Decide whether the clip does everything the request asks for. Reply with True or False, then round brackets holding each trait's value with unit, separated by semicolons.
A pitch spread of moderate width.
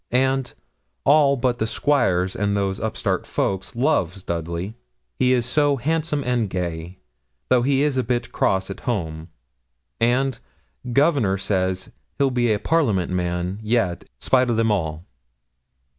False (6.0 semitones)